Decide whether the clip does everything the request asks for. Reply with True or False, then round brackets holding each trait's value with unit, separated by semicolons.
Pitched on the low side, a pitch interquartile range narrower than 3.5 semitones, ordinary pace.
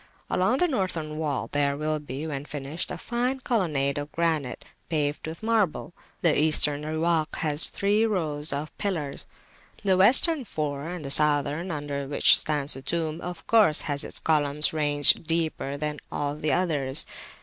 False (155 Hz; 3.1 semitones; 160 wpm)